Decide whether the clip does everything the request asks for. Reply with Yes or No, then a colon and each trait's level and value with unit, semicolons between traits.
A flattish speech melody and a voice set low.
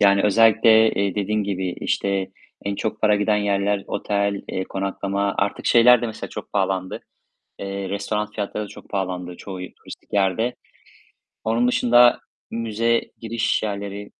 Yes: narrow, 2.1 semitones; low, 100 Hz